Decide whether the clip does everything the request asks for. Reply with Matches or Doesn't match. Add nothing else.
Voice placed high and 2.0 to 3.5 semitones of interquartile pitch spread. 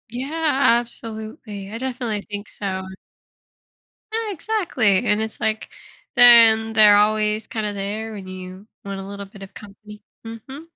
Matches